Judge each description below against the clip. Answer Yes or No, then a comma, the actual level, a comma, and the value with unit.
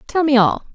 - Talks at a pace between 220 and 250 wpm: Yes, fast, 240 wpm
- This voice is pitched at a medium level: No, very high, 265 Hz